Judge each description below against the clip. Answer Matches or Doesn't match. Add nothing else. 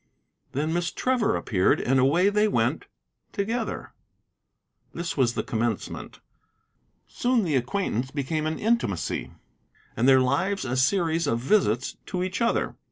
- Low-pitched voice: Doesn't match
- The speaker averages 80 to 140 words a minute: Matches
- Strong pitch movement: Matches